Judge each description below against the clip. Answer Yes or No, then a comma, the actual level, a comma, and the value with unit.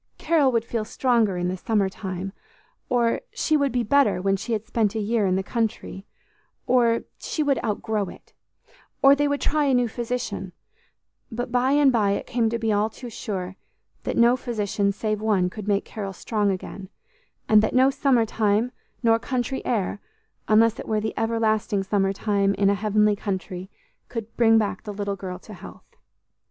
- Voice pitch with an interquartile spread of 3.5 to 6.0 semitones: No, average, 3.1 semitones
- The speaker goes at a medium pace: Yes, average, 185 wpm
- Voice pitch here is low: No, high, 220 Hz